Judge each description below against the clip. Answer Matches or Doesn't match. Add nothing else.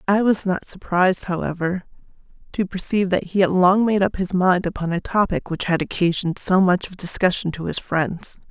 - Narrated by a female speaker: Matches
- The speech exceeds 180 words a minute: Matches